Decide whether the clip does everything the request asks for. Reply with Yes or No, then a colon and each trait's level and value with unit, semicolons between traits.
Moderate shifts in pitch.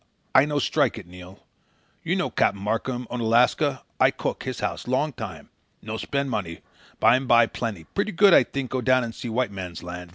Yes: average, 4.7 semitones